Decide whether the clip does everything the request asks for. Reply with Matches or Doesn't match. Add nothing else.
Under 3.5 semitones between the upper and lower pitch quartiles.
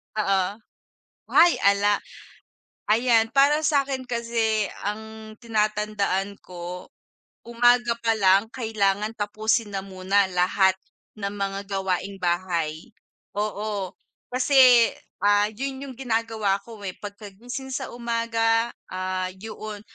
Matches